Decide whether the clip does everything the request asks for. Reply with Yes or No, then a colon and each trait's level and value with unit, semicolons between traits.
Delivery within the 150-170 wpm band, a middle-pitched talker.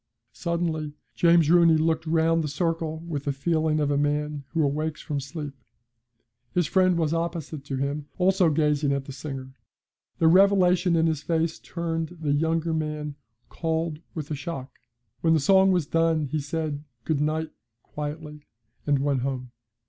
Yes: average, 165 wpm; medium, 155 Hz